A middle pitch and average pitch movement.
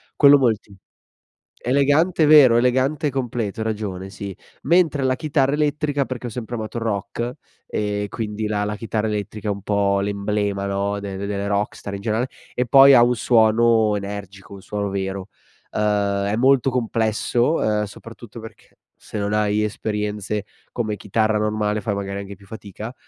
No: low, 105 Hz; average, 3.2 semitones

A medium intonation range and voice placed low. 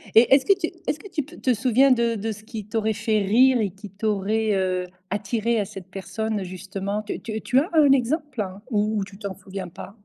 No: average, 3.7 semitones; high, 215 Hz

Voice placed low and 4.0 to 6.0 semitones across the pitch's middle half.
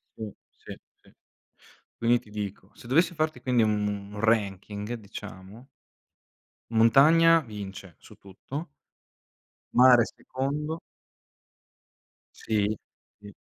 Yes: low, 110 Hz; average, 4.4 semitones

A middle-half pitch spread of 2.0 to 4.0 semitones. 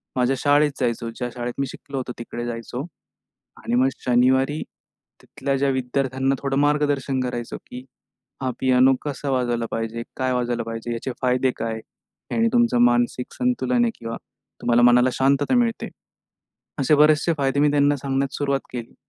Yes: average, 2.7 semitones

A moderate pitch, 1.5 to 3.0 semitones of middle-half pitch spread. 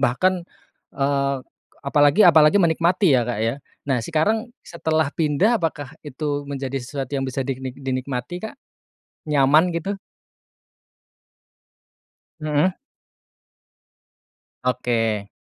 No: medium, 145 Hz; average, 3.8 semitones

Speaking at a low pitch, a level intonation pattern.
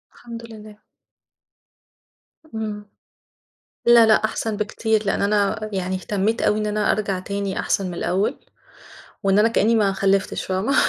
No: high, 210 Hz; narrow, 1.9 semitones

